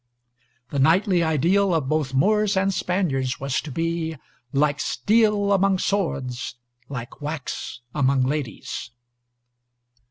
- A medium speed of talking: No, slow, 115 wpm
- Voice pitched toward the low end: No, medium, 160 Hz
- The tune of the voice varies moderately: No, wide, 6.0 semitones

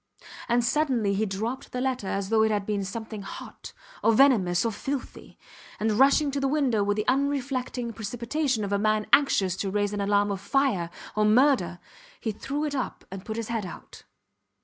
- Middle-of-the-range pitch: No, high, 220 Hz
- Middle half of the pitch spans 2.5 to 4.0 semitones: No, average, 4.6 semitones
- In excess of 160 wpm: Yes, average, 195 wpm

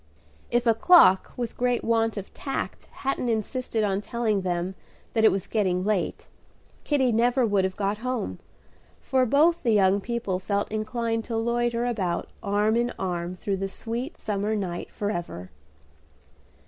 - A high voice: Yes, high, 220 Hz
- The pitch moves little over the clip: No, average, 3.6 semitones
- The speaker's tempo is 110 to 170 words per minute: Yes, average, 155 wpm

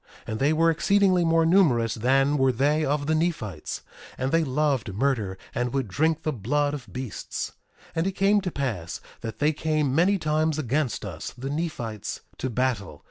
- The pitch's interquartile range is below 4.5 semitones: No, average, 4.8 semitones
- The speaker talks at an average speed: Yes, average, 185 wpm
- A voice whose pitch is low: No, medium, 145 Hz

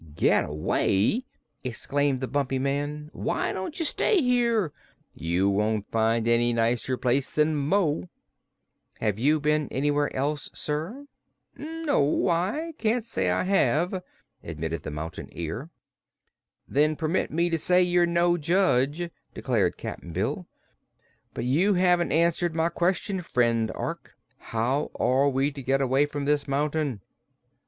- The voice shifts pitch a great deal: Yes, wide, 6.0 semitones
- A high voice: No, medium, 145 Hz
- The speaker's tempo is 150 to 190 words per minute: No, average, 140 wpm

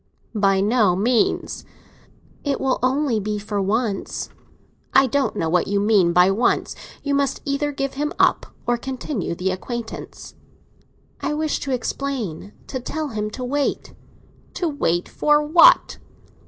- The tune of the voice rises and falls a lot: Yes, wide, 5.7 semitones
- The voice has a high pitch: Yes, high, 245 Hz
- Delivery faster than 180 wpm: No, average, 140 wpm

